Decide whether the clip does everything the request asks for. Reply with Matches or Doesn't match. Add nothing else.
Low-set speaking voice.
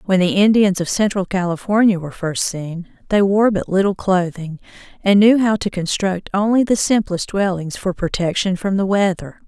Doesn't match